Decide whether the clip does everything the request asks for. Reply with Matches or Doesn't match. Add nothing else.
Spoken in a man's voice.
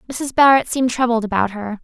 Doesn't match